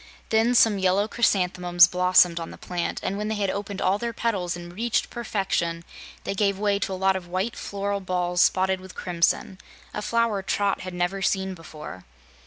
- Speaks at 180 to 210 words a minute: Yes, average, 190 wpm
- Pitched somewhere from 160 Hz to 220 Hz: Yes, high, 190 Hz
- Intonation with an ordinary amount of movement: No, narrow, 2.3 semitones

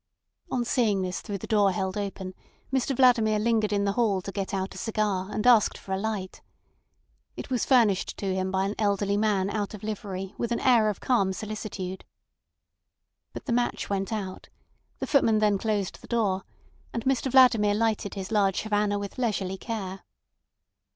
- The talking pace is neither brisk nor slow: Yes, average, 180 wpm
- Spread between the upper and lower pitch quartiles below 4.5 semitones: Yes, narrow, 2.6 semitones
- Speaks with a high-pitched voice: Yes, high, 210 Hz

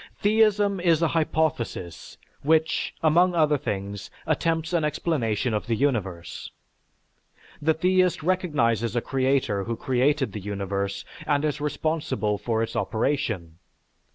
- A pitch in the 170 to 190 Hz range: No, medium, 140 Hz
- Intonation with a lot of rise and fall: Yes, wide, 6.9 semitones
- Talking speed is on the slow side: Yes, slow, 125 wpm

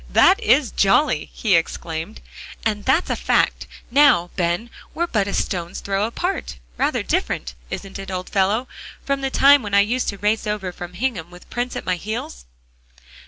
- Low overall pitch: No, high, 200 Hz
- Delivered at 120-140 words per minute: No, average, 175 wpm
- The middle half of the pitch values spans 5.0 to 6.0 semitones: Yes, wide, 5.4 semitones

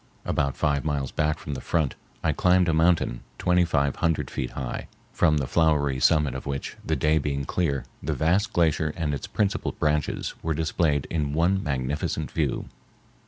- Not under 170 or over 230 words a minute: Yes, average, 175 wpm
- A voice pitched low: Yes, very low, 75 Hz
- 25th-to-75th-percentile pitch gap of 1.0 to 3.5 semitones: Yes, average, 2.9 semitones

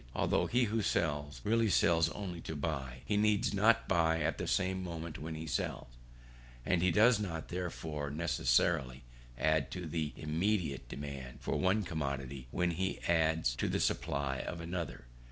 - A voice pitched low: Yes, very low, 80 Hz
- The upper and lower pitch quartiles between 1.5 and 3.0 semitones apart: No, average, 4.2 semitones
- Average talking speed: Yes, average, 165 wpm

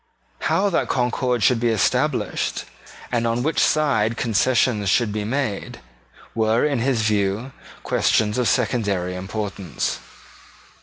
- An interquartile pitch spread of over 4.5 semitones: No, average, 3.2 semitones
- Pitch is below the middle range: Yes, low, 115 Hz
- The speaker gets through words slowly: Yes, slow, 120 wpm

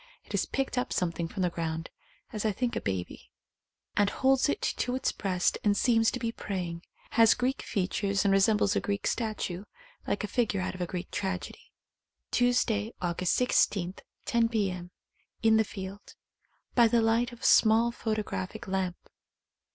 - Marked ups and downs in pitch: No, average, 4.1 semitones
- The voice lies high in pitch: Yes, high, 205 Hz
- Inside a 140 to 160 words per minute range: No, average, 175 wpm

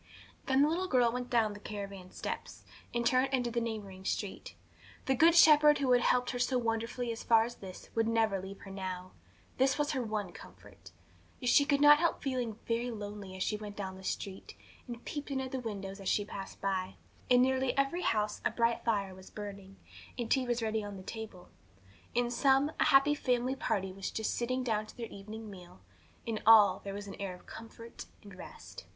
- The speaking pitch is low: No, high, 225 Hz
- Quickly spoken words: Yes, fast, 210 wpm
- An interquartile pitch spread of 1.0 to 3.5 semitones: No, average, 4.2 semitones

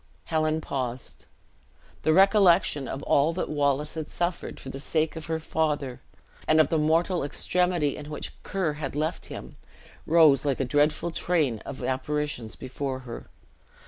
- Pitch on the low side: No, medium, 150 Hz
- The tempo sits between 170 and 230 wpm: No, average, 155 wpm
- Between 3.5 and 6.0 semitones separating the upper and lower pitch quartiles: No, average, 2.8 semitones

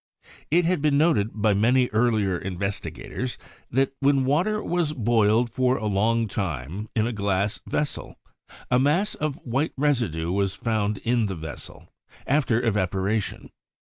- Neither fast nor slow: Yes, average, 150 wpm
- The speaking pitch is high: No, low, 115 Hz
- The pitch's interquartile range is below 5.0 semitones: No, average, 5.3 semitones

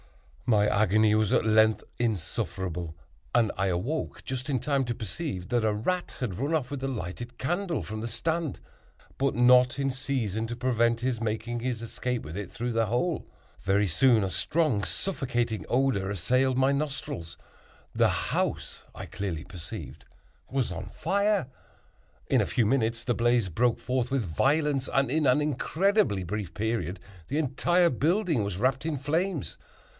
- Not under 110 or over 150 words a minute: No, average, 165 wpm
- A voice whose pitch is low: Yes, low, 120 Hz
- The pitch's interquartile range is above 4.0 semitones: Yes, average, 4.5 semitones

